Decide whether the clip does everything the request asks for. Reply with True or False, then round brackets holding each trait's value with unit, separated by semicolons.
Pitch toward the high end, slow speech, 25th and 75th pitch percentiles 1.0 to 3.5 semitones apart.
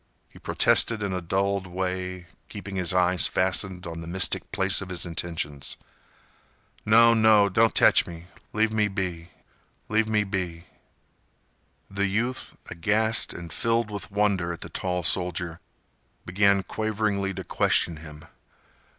False (95 Hz; 125 wpm; 3.0 semitones)